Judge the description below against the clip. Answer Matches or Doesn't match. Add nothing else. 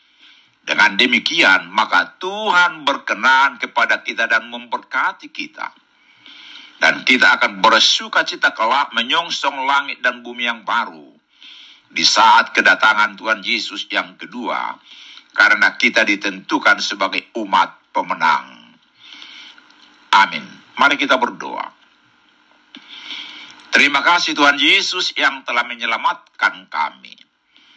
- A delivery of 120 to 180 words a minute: Doesn't match